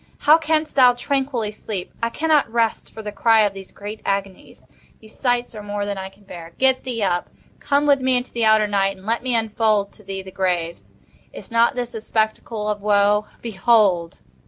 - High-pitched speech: Yes, high, 215 Hz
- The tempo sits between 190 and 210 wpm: Yes, average, 200 wpm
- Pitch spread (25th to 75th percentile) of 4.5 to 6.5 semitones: No, average, 3.4 semitones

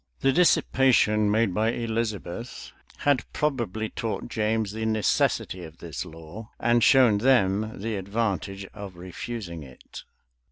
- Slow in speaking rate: Yes, slow, 130 wpm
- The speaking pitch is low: Yes, low, 110 Hz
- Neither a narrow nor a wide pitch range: Yes, average, 3.4 semitones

